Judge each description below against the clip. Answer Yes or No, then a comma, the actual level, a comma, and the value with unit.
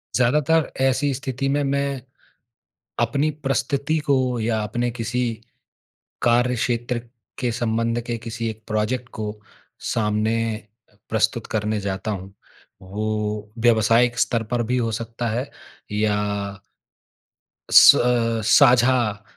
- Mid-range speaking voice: No, low, 120 Hz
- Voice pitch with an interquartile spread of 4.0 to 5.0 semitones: No, narrow, 2.4 semitones